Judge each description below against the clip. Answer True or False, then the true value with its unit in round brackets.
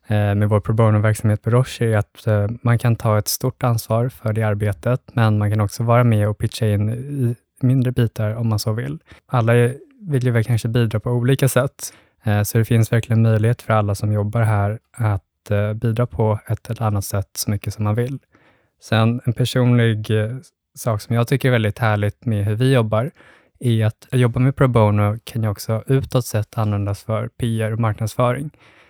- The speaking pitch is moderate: False (115 Hz)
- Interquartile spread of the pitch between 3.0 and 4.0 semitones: False (2.4 semitones)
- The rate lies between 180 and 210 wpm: True (195 wpm)